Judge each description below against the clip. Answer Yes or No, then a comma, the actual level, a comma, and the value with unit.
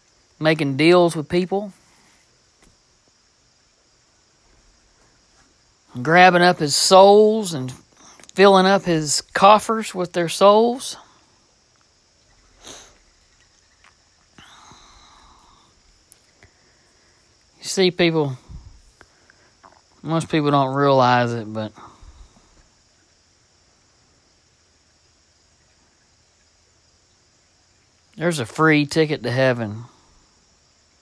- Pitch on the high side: No, low, 130 Hz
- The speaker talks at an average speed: No, slow, 60 wpm